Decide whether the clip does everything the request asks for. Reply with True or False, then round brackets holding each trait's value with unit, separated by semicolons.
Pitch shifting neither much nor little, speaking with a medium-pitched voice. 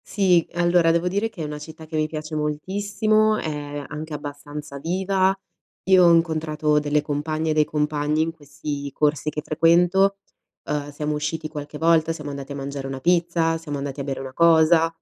False (2.3 semitones; 155 Hz)